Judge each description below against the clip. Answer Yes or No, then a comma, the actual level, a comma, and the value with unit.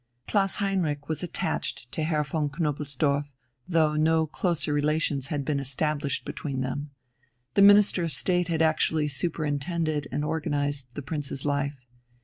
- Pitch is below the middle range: No, medium, 150 Hz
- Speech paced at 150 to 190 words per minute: No, average, 140 wpm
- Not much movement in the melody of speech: Yes, narrow, 2.2 semitones